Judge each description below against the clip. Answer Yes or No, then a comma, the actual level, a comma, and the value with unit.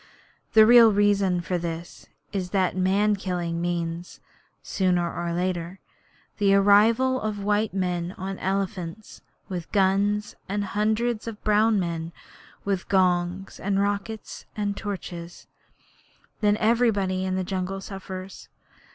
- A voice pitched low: No, high, 195 Hz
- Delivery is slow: Yes, slow, 125 wpm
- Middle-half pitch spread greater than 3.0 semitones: No, narrow, 2.4 semitones